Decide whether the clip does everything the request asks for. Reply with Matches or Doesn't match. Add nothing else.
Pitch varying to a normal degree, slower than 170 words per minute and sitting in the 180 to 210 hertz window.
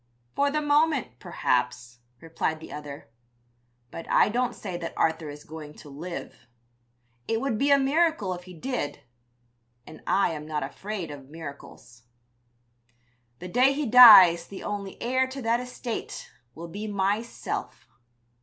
Doesn't match